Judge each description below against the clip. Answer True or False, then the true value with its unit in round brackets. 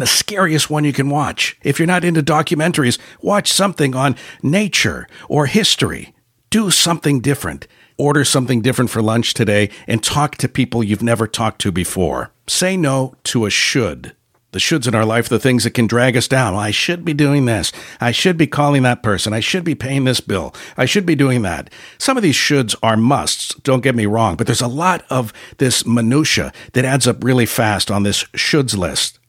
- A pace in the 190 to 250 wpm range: True (205 wpm)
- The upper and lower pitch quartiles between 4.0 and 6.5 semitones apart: True (4.7 semitones)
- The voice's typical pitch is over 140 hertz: False (130 Hz)